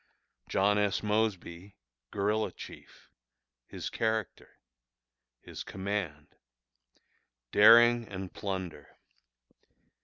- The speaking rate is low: Yes, slow, 70 wpm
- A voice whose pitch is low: Yes, low, 105 Hz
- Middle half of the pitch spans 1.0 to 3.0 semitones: Yes, narrow, 2.4 semitones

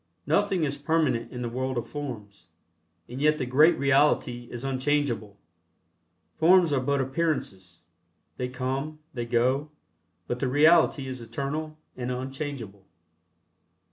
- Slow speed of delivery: Yes, slow, 130 wpm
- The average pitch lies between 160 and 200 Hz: No, low, 135 Hz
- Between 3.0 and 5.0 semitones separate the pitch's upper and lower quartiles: Yes, average, 3.4 semitones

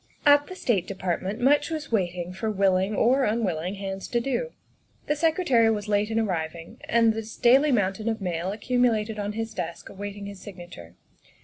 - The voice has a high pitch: Yes, high, 210 Hz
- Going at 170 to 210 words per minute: Yes, average, 180 wpm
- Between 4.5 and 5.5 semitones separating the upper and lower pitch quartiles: No, average, 4.0 semitones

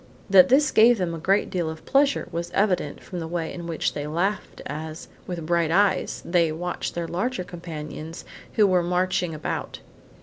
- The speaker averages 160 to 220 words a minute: Yes, average, 180 wpm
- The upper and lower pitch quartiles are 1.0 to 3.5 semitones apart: Yes, average, 2.7 semitones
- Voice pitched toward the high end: No, medium, 175 Hz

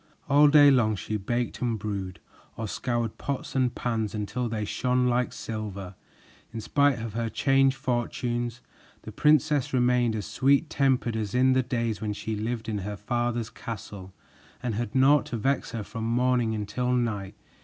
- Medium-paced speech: Yes, average, 170 wpm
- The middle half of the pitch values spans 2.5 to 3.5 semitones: Yes, average, 2.8 semitones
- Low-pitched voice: Yes, low, 120 Hz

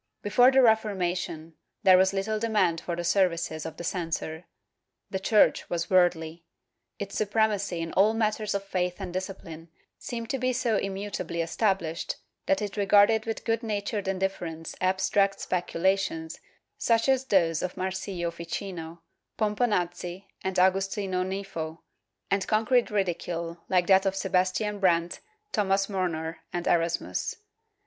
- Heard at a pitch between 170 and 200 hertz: Yes, high, 190 Hz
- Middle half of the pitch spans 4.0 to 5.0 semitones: No, average, 3.1 semitones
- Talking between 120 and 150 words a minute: Yes, average, 140 wpm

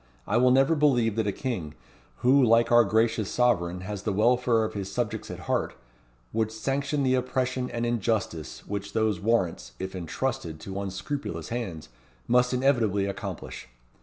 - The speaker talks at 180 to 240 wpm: No, average, 160 wpm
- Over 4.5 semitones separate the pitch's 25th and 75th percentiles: No, average, 4.2 semitones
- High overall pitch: No, low, 115 Hz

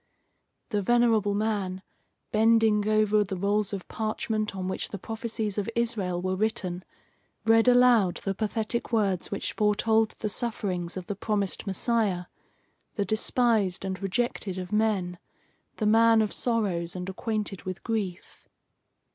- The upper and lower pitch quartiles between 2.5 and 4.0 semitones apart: Yes, average, 2.8 semitones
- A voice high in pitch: Yes, high, 210 Hz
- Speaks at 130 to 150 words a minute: Yes, average, 140 wpm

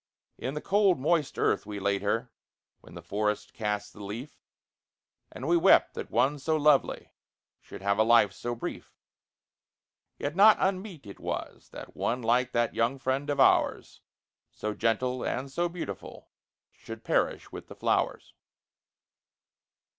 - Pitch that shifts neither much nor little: No, wide, 6.0 semitones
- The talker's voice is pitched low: Yes, low, 125 Hz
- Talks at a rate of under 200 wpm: Yes, average, 150 wpm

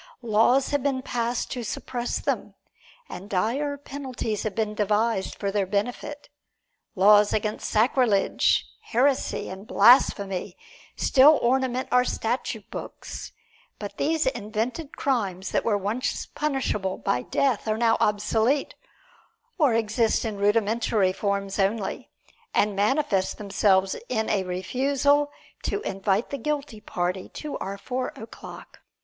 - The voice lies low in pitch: No, high, 220 Hz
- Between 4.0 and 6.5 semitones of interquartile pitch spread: Yes, average, 4.4 semitones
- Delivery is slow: Yes, slow, 125 wpm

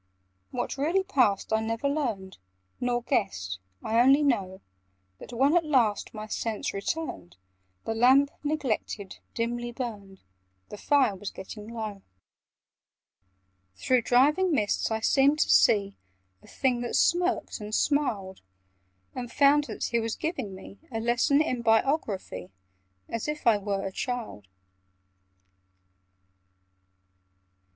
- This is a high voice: Yes, high, 235 Hz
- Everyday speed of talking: No, slow, 125 wpm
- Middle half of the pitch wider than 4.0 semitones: Yes, average, 5.2 semitones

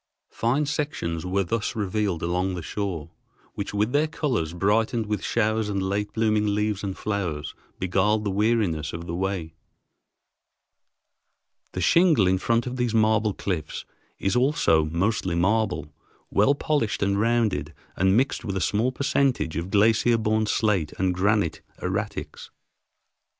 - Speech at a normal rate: Yes, average, 145 wpm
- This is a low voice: Yes, low, 105 Hz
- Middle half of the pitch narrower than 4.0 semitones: Yes, average, 3.5 semitones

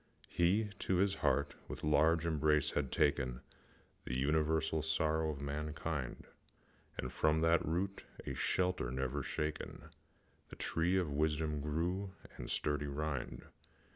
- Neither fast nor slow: No, slow, 130 wpm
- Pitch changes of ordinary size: No, narrow, 2.3 semitones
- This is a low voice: Yes, very low, 75 Hz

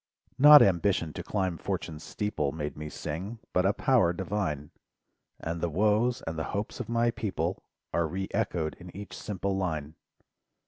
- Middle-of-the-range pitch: No, very low, 90 Hz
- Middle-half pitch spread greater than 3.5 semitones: Yes, average, 4.5 semitones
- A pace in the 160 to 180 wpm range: Yes, average, 165 wpm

